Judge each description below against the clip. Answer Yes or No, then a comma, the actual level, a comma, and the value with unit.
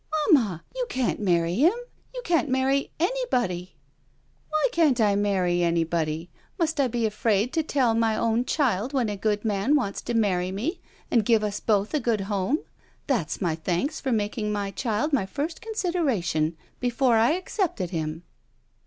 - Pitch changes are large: Yes, wide, 6.5 semitones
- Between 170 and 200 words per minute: Yes, average, 180 wpm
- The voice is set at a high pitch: Yes, high, 225 Hz